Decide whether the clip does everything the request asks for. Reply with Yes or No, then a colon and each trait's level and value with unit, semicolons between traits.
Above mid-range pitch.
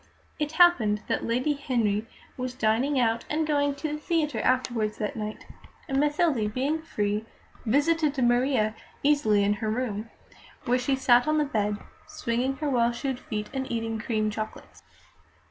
Yes: very high, 250 Hz